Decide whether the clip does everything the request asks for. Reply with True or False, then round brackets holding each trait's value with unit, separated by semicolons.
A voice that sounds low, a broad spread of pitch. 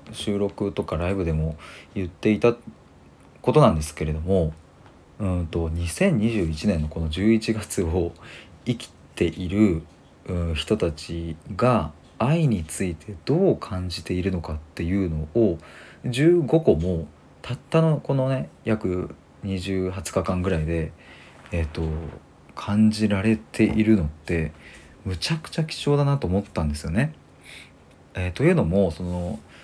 False (90 Hz; 5.0 semitones)